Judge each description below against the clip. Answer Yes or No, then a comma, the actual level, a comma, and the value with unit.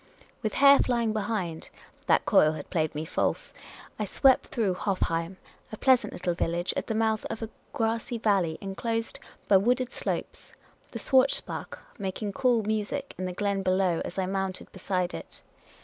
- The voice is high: Yes, high, 205 Hz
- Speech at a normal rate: Yes, average, 165 wpm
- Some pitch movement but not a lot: Yes, average, 3.8 semitones